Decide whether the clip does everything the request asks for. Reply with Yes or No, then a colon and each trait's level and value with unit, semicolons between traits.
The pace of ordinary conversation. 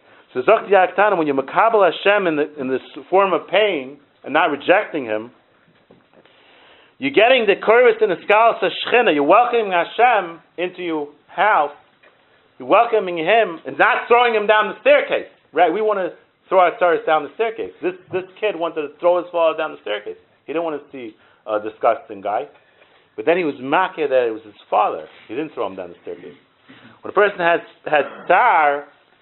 Yes: average, 185 wpm